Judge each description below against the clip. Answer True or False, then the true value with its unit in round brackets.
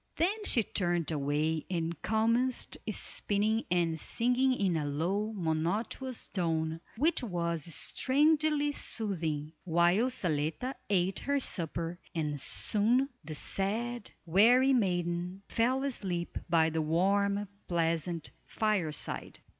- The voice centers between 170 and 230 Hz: True (185 Hz)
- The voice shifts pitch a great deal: True (6.1 semitones)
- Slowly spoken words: True (110 wpm)